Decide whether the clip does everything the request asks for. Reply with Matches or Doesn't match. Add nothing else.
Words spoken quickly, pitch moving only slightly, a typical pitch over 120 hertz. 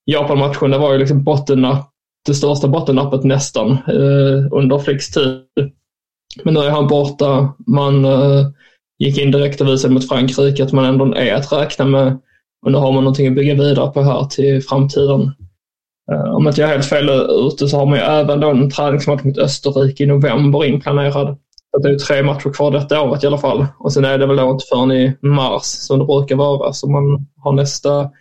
Matches